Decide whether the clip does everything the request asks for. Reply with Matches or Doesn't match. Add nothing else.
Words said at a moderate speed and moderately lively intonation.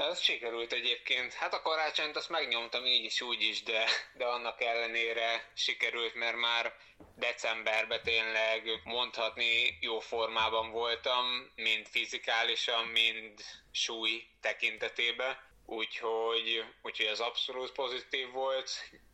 Doesn't match